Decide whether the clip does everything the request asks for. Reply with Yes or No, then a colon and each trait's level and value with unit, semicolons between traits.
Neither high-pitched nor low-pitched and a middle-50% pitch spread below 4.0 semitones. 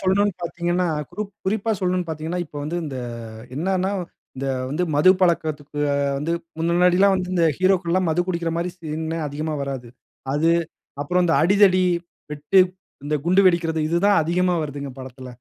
Yes: medium, 170 Hz; average, 3.2 semitones